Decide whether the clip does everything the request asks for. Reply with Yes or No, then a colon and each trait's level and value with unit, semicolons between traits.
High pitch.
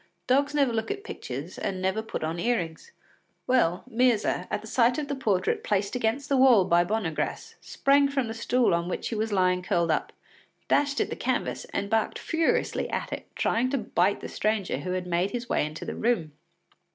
Yes: high, 220 Hz